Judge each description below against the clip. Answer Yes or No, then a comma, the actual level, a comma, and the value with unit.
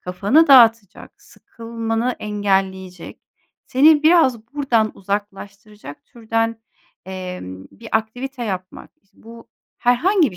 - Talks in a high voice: Yes, high, 225 Hz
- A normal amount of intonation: Yes, average, 3.9 semitones